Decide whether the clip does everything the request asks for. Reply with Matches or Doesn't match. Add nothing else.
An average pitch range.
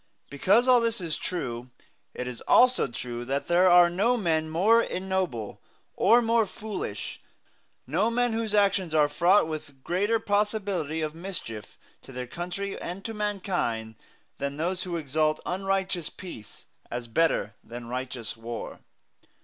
Doesn't match